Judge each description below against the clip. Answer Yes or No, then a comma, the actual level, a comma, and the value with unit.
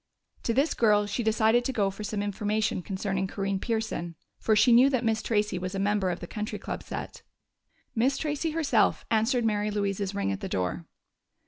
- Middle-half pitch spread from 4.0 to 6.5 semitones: No, average, 2.7 semitones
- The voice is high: Yes, high, 210 Hz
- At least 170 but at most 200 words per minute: Yes, average, 195 wpm